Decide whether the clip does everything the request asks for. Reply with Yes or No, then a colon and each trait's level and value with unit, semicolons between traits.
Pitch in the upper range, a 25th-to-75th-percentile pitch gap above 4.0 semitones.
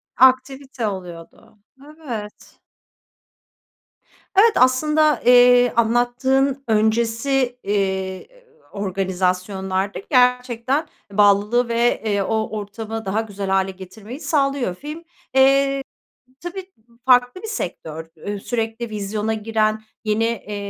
Yes: high, 225 Hz; average, 4.4 semitones